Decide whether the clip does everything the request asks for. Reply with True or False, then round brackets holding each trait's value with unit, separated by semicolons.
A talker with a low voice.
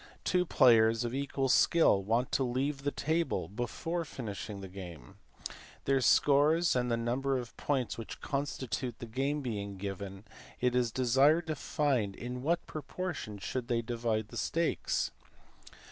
True (125 Hz)